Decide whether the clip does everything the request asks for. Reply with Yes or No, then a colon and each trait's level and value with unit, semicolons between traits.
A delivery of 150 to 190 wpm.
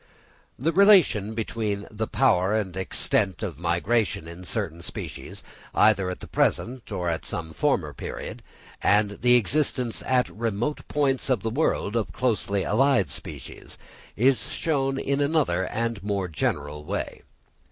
No: average, 140 wpm